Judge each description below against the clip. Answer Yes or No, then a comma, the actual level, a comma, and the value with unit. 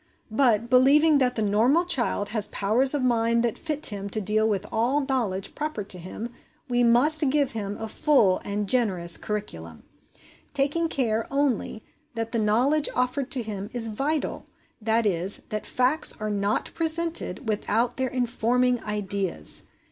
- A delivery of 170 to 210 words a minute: No, average, 155 wpm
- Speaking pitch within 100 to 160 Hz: No, high, 235 Hz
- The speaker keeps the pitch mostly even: No, average, 4.5 semitones